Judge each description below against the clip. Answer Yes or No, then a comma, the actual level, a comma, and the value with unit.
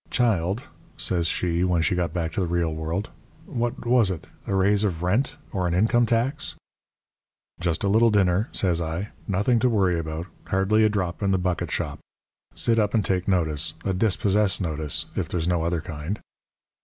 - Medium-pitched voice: No, very low, 95 Hz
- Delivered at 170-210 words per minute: Yes, average, 180 wpm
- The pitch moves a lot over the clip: No, average, 3.7 semitones